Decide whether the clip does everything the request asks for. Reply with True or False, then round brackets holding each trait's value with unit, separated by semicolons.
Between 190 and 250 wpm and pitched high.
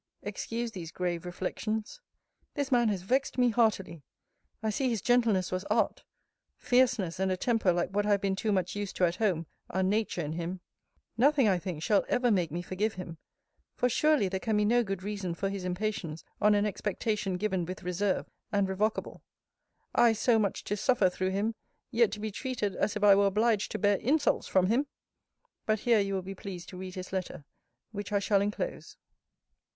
True (200 wpm; 200 Hz)